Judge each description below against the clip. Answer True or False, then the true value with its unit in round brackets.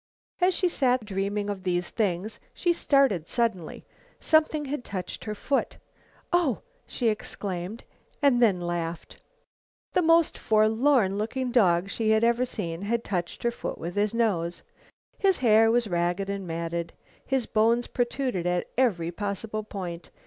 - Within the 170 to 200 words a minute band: False (145 wpm)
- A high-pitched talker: True (215 Hz)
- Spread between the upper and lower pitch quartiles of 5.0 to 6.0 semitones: True (5.4 semitones)